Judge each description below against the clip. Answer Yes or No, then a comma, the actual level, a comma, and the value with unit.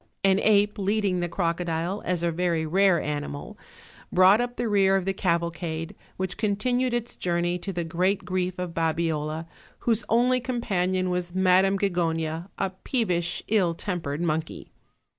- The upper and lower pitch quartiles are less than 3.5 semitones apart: Yes, average, 2.9 semitones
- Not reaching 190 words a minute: Yes, average, 155 wpm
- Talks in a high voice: No, medium, 180 Hz